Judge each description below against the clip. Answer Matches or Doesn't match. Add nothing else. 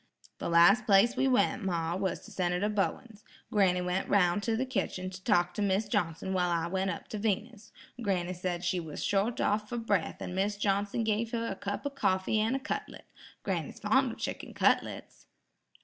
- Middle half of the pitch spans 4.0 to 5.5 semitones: Doesn't match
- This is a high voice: Matches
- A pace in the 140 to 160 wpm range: Doesn't match